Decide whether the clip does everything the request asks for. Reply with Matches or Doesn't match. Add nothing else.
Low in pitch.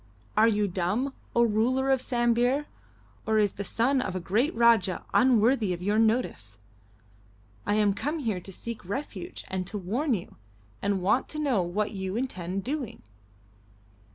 Doesn't match